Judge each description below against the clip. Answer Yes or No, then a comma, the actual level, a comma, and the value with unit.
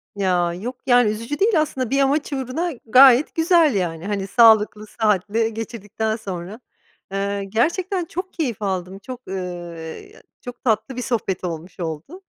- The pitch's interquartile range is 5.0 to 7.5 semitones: Yes, wide, 5.6 semitones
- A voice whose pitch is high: Yes, high, 220 Hz